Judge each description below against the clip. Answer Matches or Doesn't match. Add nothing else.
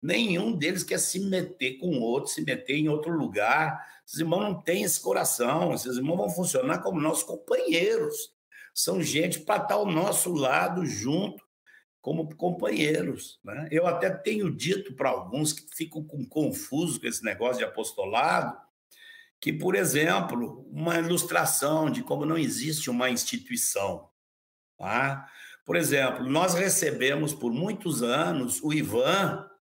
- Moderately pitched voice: Matches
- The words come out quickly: Doesn't match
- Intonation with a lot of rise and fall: Doesn't match